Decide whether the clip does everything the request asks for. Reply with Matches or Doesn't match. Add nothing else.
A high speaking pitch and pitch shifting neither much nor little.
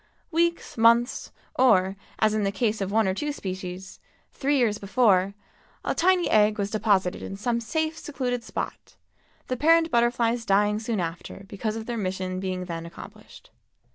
Matches